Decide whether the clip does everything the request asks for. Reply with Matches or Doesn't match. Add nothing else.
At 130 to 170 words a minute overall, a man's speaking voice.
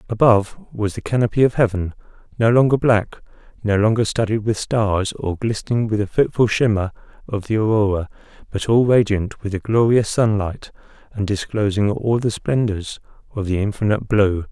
Matches